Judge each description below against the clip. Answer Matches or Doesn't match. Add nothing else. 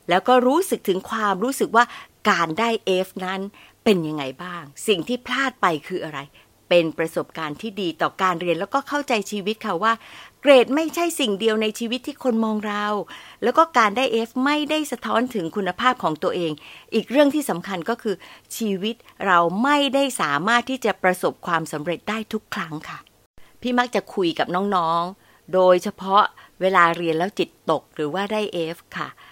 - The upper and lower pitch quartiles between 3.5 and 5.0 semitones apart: Doesn't match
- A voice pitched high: Matches